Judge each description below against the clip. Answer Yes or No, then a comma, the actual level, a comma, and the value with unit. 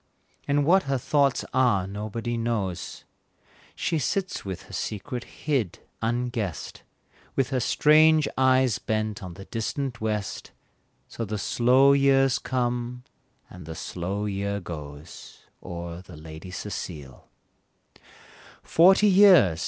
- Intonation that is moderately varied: No, wide, 5.9 semitones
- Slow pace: Yes, slow, 120 wpm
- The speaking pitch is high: No, low, 115 Hz